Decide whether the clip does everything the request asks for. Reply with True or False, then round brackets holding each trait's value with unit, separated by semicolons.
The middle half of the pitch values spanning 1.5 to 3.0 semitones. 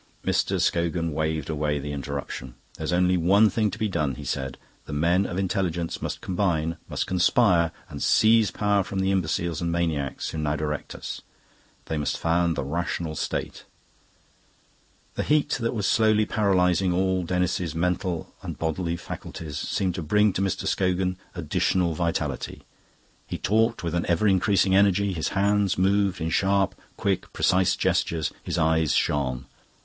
False (3.4 semitones)